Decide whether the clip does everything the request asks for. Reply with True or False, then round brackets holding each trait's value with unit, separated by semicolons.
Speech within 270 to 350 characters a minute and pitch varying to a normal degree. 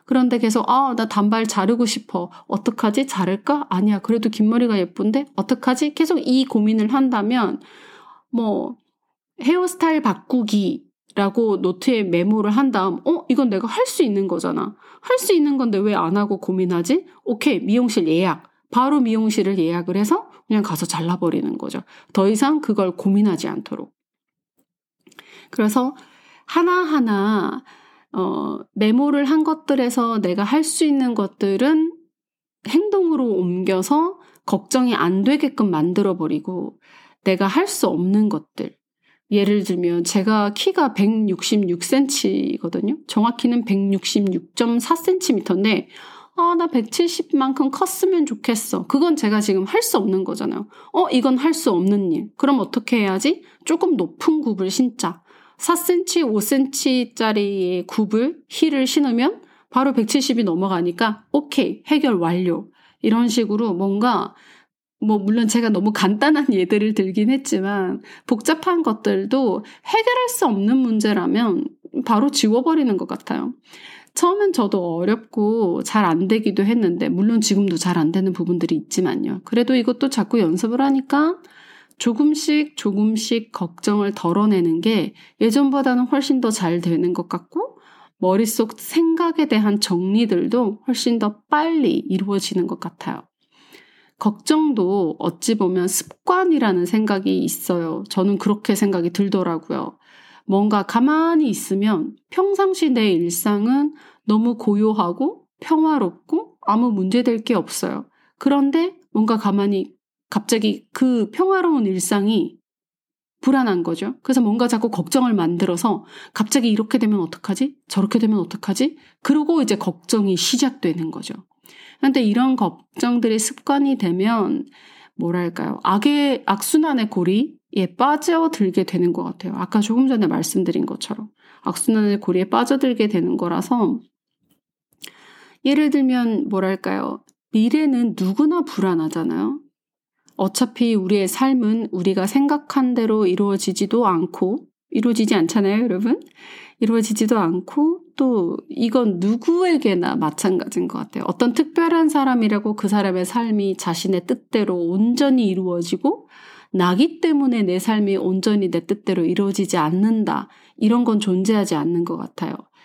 False (290 characters per minute; 6.4 semitones)